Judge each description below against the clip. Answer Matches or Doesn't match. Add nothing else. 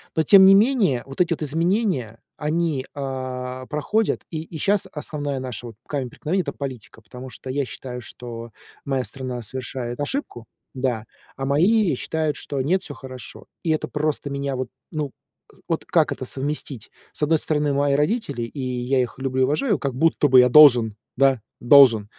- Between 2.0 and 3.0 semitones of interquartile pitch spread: Doesn't match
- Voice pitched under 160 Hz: Matches